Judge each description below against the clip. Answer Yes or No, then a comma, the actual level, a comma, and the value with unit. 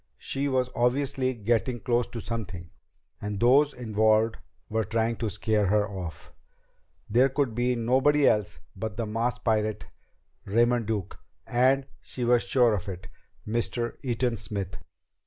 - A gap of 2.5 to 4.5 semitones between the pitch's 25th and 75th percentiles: Yes, average, 2.8 semitones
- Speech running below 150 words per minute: Yes, average, 140 wpm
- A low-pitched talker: Yes, low, 115 Hz